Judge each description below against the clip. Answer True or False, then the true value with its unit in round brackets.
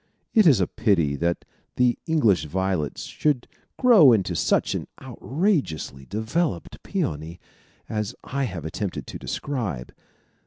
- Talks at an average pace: False (125 wpm)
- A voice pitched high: False (105 Hz)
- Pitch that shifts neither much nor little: False (8.4 semitones)